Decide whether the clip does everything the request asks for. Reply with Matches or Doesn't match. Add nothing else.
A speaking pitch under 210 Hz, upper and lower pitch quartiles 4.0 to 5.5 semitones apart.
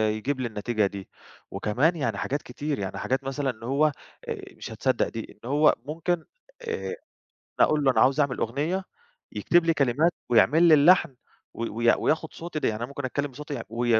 Matches